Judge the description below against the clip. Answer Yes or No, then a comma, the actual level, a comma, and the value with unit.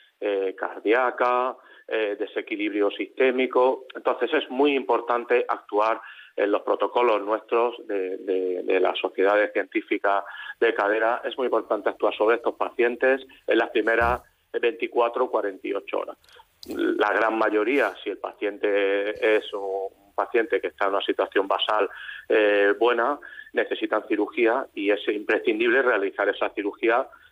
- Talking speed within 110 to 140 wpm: Yes, average, 130 wpm